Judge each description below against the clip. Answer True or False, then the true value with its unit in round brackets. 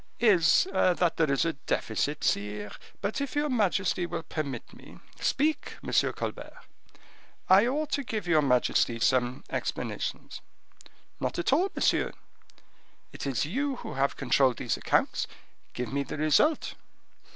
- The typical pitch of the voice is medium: True (165 Hz)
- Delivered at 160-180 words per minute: False (140 wpm)